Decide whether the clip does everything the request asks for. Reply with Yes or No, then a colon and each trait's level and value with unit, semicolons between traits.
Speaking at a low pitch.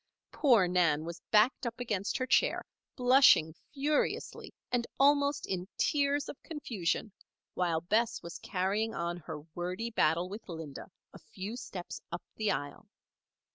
No: high, 205 Hz